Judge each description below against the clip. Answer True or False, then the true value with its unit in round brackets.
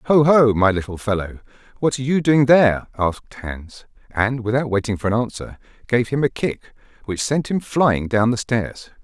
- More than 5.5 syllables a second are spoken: False (5.1 syllables/s)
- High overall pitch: False (120 Hz)